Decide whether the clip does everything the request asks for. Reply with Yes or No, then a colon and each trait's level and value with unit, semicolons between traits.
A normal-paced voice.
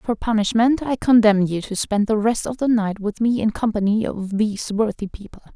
No: fast, 215 wpm